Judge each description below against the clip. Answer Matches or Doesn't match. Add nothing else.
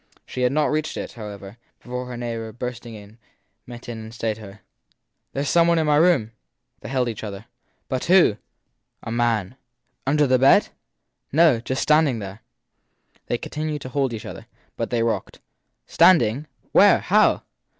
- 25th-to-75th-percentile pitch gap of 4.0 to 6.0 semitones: Matches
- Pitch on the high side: Doesn't match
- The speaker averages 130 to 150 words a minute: Doesn't match